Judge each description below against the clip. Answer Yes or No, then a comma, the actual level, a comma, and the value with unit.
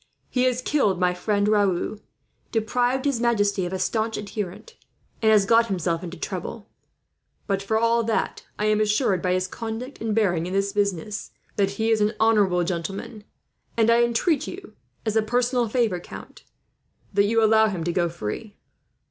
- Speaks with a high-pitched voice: Yes, high, 210 Hz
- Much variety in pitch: No, average, 3.3 semitones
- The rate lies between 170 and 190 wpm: Yes, average, 175 wpm